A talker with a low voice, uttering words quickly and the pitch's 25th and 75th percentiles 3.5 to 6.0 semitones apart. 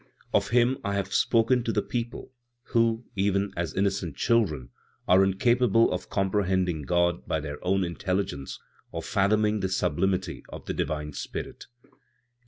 No: very low, 95 Hz; average, 150 wpm; average, 4.2 semitones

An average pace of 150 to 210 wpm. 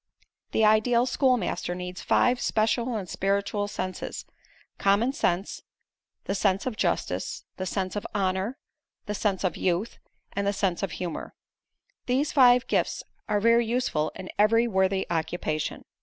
No: average, 140 wpm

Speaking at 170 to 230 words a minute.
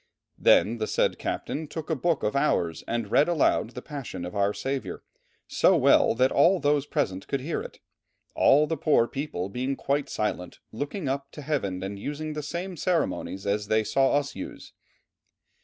Yes: average, 180 wpm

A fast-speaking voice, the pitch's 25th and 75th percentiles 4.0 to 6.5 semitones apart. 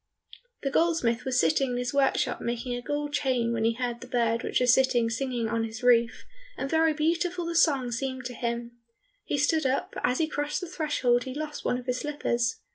No: fast, 215 wpm; average, 3.6 semitones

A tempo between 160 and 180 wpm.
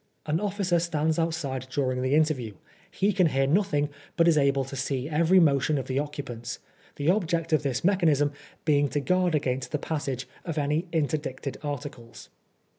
Yes: average, 175 wpm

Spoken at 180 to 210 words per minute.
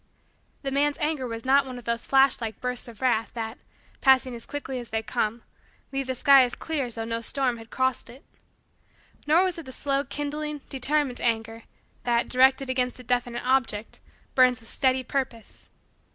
Yes: average, 185 wpm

